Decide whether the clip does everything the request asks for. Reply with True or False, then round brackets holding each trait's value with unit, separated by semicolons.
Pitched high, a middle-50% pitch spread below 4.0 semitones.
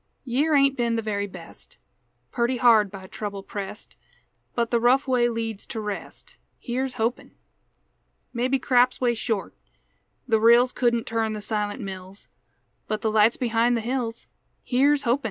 True (235 Hz; 2.6 semitones)